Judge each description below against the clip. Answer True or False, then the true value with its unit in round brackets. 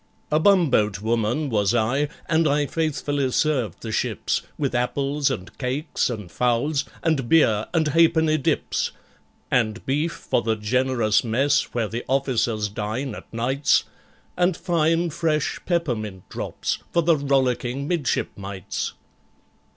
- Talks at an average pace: False (130 wpm)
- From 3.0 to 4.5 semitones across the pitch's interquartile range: False (5.3 semitones)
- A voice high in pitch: False (135 Hz)